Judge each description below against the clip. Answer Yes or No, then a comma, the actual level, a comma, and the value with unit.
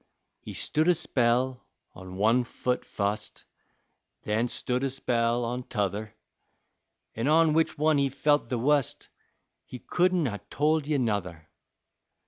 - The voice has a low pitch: Yes, low, 125 Hz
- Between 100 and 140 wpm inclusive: Yes, slow, 135 wpm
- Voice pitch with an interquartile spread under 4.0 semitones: No, average, 5.1 semitones